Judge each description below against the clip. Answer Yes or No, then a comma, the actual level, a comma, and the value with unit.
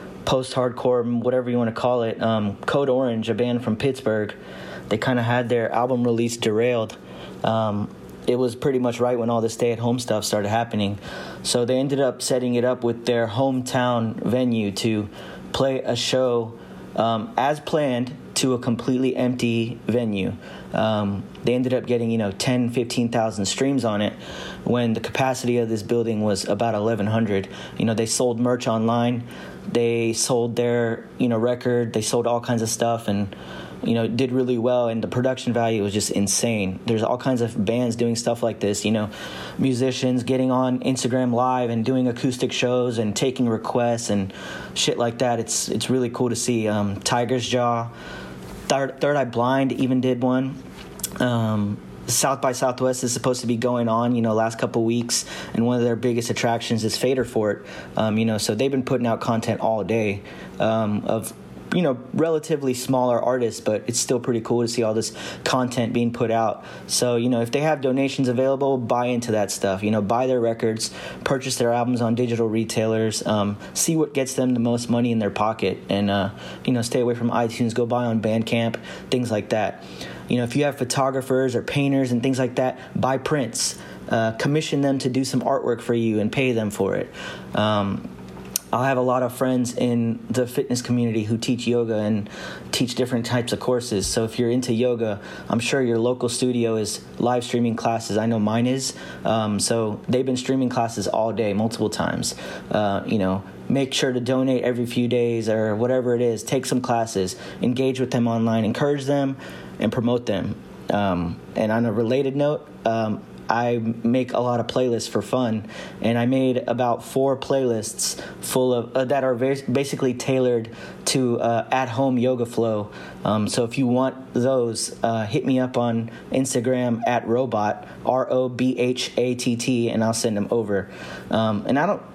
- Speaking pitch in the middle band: No, low, 120 Hz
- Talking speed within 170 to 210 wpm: Yes, average, 195 wpm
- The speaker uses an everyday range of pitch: No, narrow, 2.2 semitones